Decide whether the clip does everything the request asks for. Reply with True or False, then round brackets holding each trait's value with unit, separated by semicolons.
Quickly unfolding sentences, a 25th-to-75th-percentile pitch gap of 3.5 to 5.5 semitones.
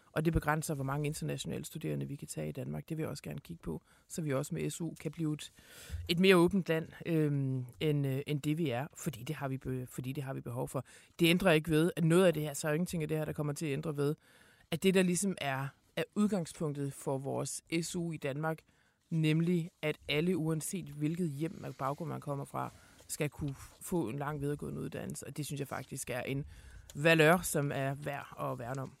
False (240 wpm; 3.0 semitones)